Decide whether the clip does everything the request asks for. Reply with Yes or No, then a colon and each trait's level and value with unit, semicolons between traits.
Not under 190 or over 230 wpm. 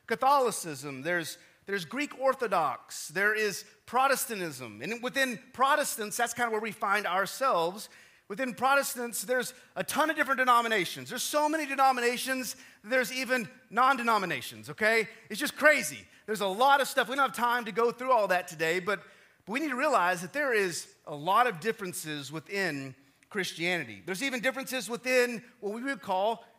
No: average, 170 wpm